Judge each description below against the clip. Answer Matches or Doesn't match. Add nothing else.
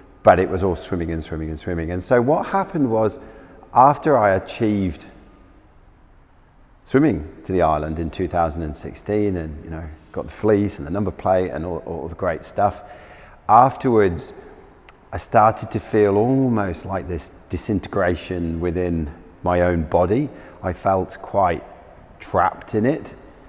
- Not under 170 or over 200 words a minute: Doesn't match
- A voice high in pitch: Doesn't match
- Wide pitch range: Doesn't match